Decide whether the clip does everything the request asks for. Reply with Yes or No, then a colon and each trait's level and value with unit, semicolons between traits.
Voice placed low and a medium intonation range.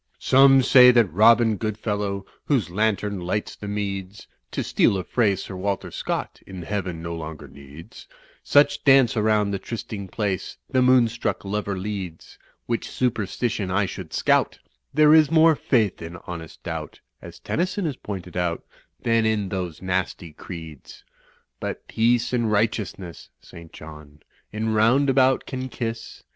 Yes: low, 105 Hz; average, 4.3 semitones